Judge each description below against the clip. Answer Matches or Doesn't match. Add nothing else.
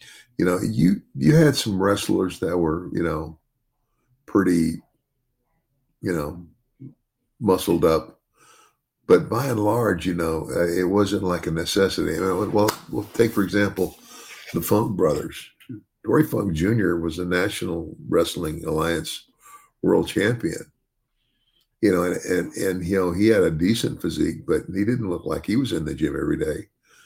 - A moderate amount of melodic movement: Doesn't match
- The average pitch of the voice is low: Matches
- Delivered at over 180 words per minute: Doesn't match